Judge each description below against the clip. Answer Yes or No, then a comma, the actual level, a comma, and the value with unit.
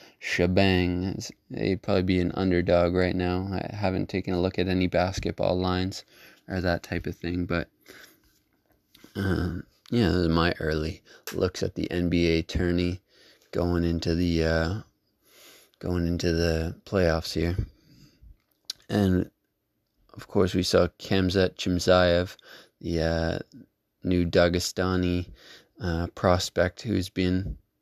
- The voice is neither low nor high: No, very low, 90 Hz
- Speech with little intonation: Yes, narrow, 1.3 semitones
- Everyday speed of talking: No, slow, 125 wpm